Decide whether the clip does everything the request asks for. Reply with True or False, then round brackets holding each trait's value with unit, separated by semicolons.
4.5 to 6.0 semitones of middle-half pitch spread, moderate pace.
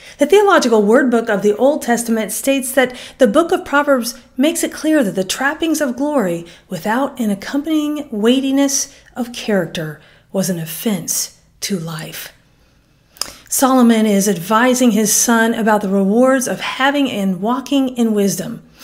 True (5.1 semitones; 150 wpm)